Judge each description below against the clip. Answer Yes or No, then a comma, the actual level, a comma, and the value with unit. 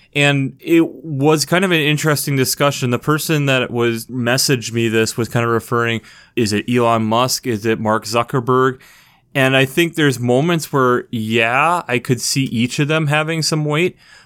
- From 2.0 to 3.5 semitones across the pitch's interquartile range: No, average, 4.1 semitones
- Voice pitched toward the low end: Yes, low, 130 Hz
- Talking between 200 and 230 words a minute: No, average, 180 wpm